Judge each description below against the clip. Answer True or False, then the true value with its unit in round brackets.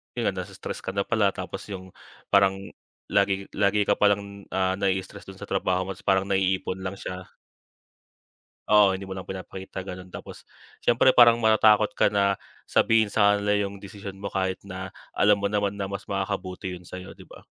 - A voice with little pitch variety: True (1.3 semitones)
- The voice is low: True (100 Hz)